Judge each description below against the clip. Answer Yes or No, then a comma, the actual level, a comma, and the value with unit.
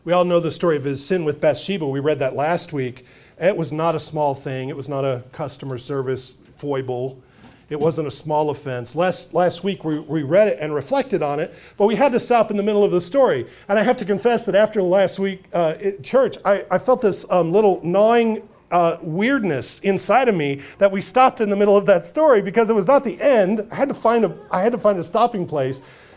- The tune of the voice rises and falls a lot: Yes, wide, 5.9 semitones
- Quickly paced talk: Yes, fast, 245 wpm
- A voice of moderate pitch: Yes, medium, 180 Hz